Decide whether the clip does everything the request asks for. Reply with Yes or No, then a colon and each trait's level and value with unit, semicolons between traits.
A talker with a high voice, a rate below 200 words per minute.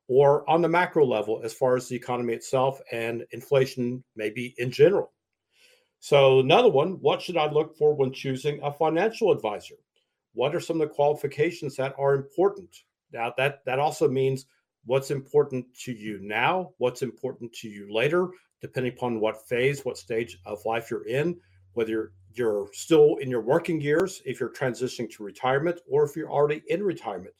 No: low, 135 Hz; average, 180 wpm